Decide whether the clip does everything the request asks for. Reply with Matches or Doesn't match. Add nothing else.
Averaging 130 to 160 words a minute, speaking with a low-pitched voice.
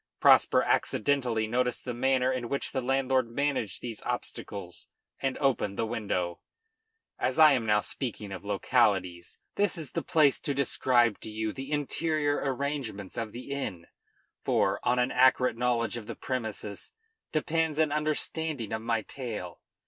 Matches